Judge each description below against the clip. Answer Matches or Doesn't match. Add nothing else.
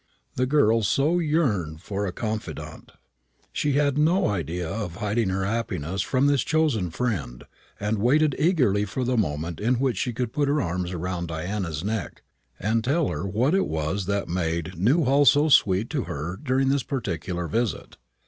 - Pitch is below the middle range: Matches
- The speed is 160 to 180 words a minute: Matches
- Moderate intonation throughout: Doesn't match